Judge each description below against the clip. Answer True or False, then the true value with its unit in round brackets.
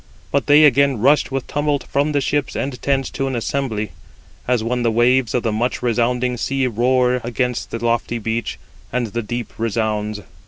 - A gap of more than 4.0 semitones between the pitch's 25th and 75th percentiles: False (2.7 semitones)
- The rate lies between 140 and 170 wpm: False (185 wpm)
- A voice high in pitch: False (125 Hz)